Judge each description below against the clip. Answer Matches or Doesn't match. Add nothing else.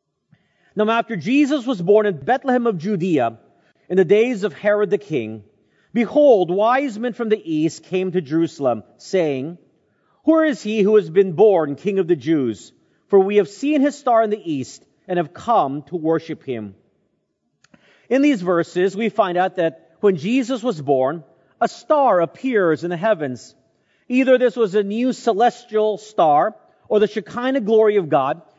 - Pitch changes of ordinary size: Doesn't match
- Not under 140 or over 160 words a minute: Doesn't match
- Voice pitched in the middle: Doesn't match